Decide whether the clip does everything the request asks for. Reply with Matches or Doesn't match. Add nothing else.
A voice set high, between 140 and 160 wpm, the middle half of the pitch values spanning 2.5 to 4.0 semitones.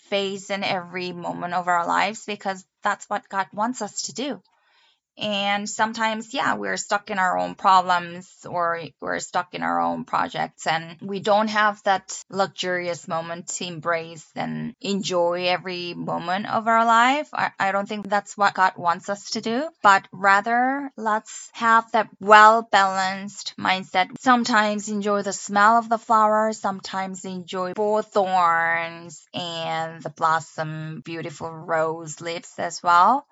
Matches